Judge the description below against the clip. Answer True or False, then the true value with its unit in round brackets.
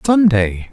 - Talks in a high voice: False (150 Hz)